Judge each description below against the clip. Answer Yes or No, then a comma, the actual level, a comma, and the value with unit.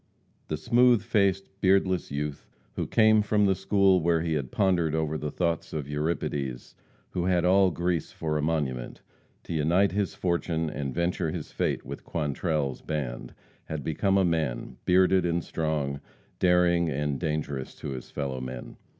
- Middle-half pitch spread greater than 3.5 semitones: Yes, average, 3.9 semitones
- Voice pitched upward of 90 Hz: No, very low, 80 Hz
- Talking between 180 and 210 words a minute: No, average, 160 wpm